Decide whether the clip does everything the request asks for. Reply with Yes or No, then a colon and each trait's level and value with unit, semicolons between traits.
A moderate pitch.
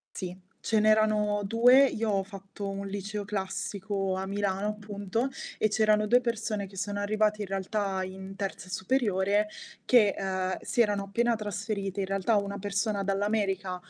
No: high, 205 Hz